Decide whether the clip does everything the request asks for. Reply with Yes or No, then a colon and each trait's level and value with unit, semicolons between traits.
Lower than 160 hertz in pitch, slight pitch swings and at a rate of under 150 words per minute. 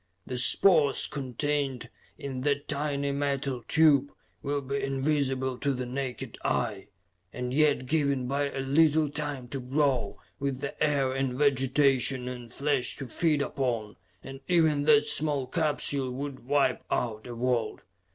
Yes: low, 135 Hz; narrow, 2.3 semitones; average, 140 wpm